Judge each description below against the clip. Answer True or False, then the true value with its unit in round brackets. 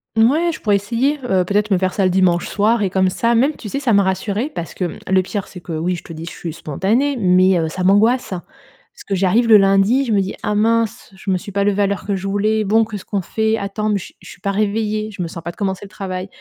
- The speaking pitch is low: False (200 Hz)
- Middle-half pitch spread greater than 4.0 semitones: False (2.8 semitones)